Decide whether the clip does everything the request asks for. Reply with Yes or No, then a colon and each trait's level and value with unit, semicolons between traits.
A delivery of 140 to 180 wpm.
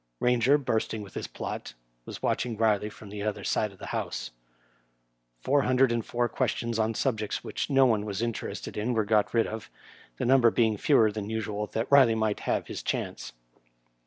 No: average, 190 wpm